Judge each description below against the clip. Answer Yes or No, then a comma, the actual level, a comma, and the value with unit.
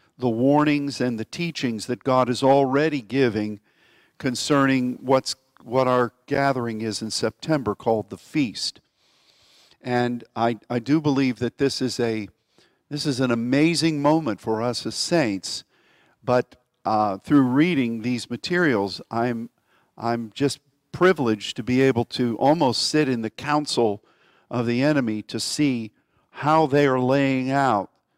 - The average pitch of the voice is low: Yes, low, 125 Hz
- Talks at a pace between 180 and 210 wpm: No, average, 145 wpm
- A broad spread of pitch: No, average, 3.5 semitones